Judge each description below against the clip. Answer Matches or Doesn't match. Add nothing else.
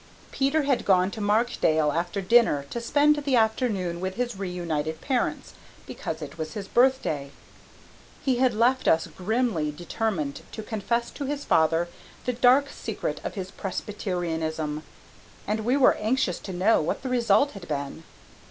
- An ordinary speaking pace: Matches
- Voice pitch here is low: Doesn't match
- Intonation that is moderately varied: Doesn't match